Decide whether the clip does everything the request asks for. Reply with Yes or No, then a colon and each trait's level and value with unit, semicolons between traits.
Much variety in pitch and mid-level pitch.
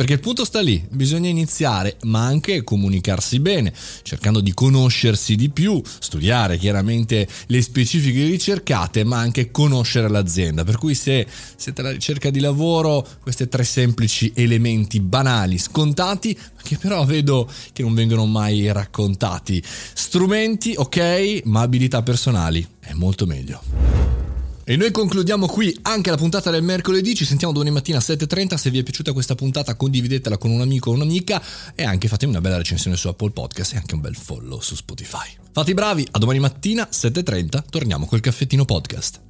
No: wide, 6.3 semitones; low, 125 Hz